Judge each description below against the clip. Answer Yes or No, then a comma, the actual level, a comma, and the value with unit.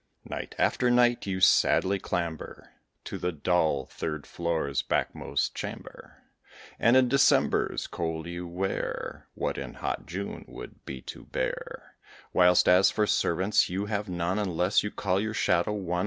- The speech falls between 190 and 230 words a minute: No, average, 150 wpm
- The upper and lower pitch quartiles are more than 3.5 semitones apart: No, average, 3.2 semitones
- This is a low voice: Yes, very low, 90 Hz